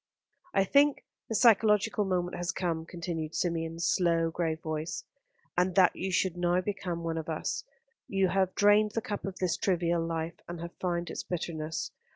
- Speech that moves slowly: No, average, 175 wpm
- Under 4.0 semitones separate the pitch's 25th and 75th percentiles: Yes, narrow, 2.5 semitones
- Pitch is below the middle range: No, medium, 175 Hz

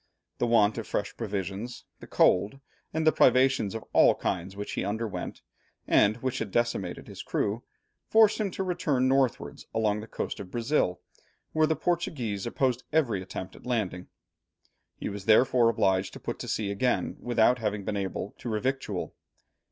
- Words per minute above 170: No, average, 165 wpm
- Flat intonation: No, average, 4.3 semitones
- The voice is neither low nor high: No, low, 115 Hz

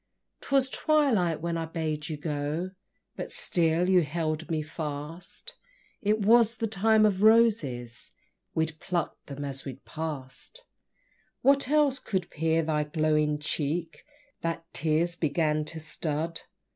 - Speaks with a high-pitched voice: No, medium, 165 Hz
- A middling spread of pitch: Yes, average, 4.8 semitones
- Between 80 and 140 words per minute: Yes, slow, 135 wpm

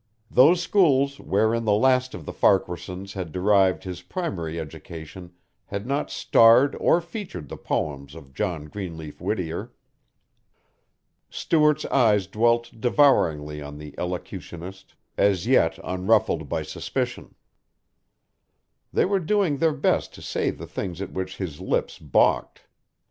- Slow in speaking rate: Yes, slow, 130 wpm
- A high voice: No, low, 100 Hz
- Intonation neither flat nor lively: No, wide, 7.7 semitones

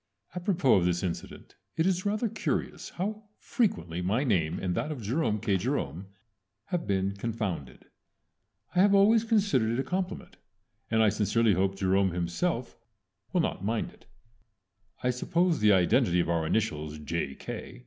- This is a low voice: Yes, low, 110 Hz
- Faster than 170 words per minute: No, average, 155 wpm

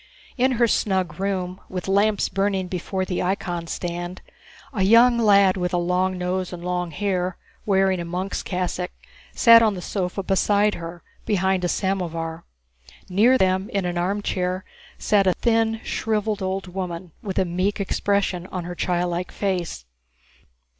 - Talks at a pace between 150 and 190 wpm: Yes, average, 155 wpm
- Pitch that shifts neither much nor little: No, narrow, 2.1 semitones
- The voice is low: No, medium, 185 Hz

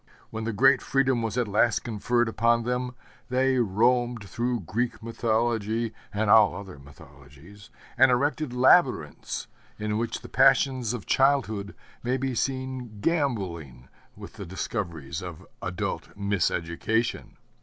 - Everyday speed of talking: No, slow, 130 wpm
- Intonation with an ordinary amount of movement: Yes, average, 3.8 semitones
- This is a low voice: Yes, low, 115 Hz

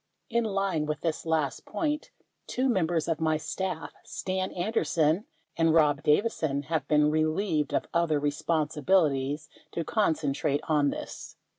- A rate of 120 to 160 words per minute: Yes, average, 140 wpm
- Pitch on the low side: No, medium, 160 Hz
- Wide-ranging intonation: No, average, 3.8 semitones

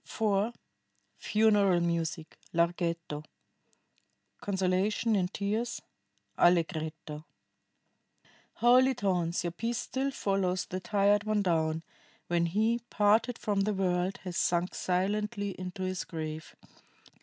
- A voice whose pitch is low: No, high, 190 Hz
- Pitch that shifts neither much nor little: Yes, average, 3.5 semitones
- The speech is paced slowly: Yes, slow, 105 wpm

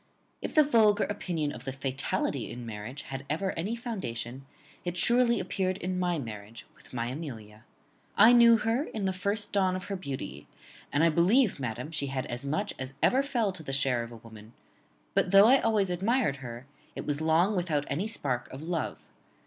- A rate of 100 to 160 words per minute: No, average, 195 wpm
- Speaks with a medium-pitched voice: Yes, medium, 165 Hz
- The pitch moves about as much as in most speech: No, wide, 7.7 semitones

